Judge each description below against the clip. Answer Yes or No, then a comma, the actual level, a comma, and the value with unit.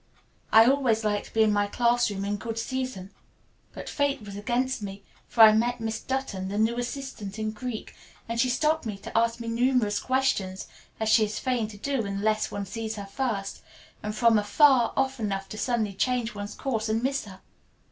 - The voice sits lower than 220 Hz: No, high, 225 Hz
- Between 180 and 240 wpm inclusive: Yes, average, 200 wpm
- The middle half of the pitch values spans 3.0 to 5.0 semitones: Yes, average, 3.3 semitones